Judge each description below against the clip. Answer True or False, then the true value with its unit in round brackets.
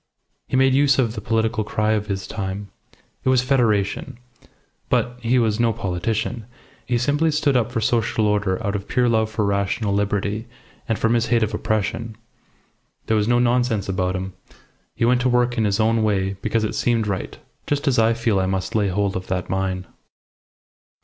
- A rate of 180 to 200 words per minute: True (190 wpm)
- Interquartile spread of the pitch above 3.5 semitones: False (3.2 semitones)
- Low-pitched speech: True (110 Hz)